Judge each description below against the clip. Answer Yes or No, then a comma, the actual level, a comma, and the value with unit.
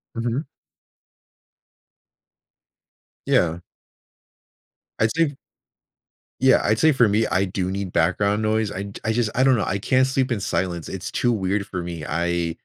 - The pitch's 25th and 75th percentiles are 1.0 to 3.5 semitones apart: No, average, 4.5 semitones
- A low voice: Yes, low, 105 Hz